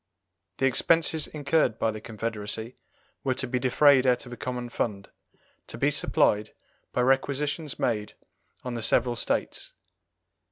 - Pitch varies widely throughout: No, average, 3.2 semitones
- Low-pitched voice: Yes, low, 125 Hz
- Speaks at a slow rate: No, average, 145 wpm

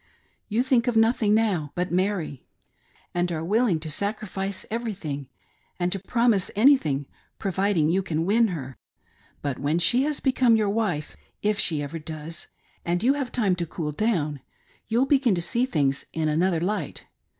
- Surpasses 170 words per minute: No, average, 165 wpm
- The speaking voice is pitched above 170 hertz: Yes, high, 190 Hz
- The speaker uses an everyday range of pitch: No, wide, 6.0 semitones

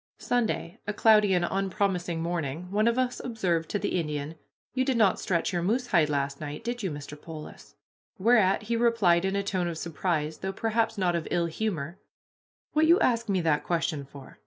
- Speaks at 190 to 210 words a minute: Yes, average, 195 wpm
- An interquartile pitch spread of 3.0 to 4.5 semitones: No, average, 5.1 semitones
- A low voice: No, medium, 185 Hz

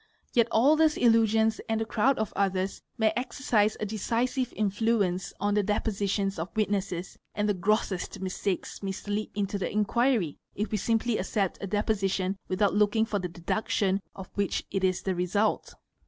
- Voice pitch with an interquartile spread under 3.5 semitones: Yes, narrow, 2.4 semitones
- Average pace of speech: Yes, average, 170 wpm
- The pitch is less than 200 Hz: No, high, 205 Hz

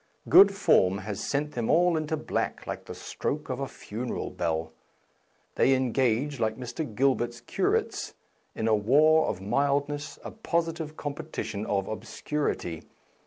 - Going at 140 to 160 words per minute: Yes, average, 150 wpm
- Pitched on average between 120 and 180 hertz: Yes, low, 135 Hz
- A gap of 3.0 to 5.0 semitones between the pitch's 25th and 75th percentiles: No, wide, 5.6 semitones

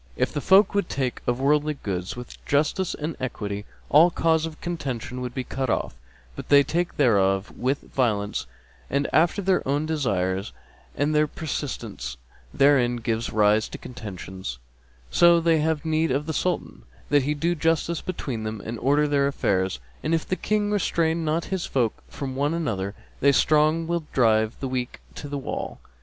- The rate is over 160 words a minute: Yes, average, 175 wpm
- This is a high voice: No, medium, 140 Hz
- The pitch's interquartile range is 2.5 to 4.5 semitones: No, wide, 5.6 semitones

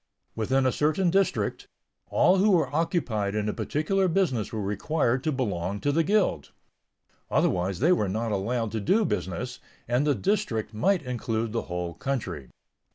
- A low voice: Yes, low, 125 Hz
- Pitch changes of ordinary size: No, wide, 7.6 semitones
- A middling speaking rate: Yes, average, 160 wpm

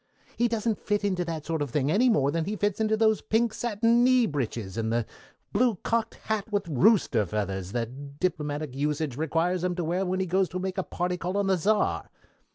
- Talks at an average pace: No, fast, 215 wpm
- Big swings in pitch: Yes, wide, 6.5 semitones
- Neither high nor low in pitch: Yes, medium, 180 Hz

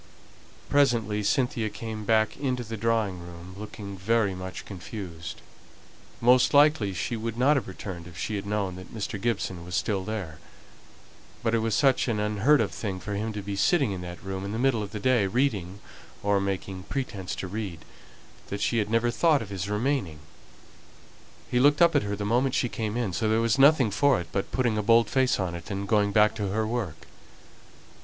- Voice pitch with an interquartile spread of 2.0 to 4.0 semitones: Yes, average, 3.5 semitones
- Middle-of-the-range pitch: No, low, 105 Hz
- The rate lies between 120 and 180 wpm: No, average, 200 wpm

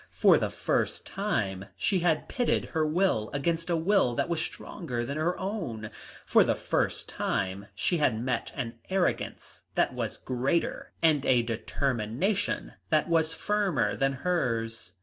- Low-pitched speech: No, medium, 145 Hz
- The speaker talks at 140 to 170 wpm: Yes, average, 150 wpm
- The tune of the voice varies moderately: No, wide, 7.1 semitones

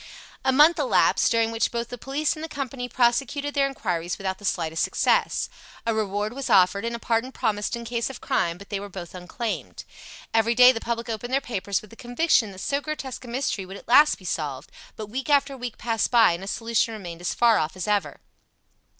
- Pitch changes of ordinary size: Yes, average, 4.5 semitones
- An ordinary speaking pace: No, fast, 220 wpm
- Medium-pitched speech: No, high, 230 Hz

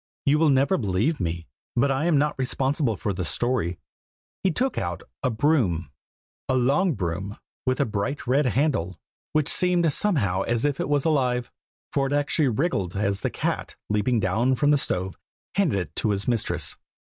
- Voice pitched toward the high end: No, low, 125 Hz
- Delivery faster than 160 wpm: Yes, average, 180 wpm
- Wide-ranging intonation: Yes, wide, 6.7 semitones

